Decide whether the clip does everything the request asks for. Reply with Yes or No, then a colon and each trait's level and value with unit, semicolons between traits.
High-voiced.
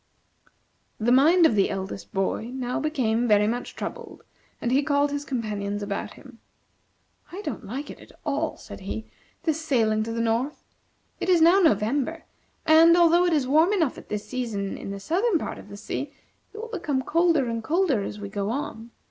Yes: very high, 260 Hz